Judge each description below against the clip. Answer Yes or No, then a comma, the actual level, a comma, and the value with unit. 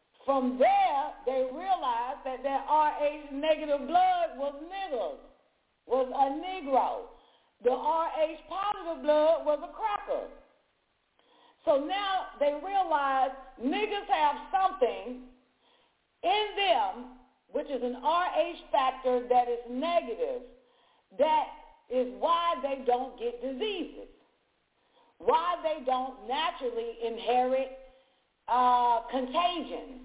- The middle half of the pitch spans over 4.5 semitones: Yes, wide, 5.4 semitones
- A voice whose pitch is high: Yes, very high, 290 Hz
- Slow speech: Yes, slow, 105 wpm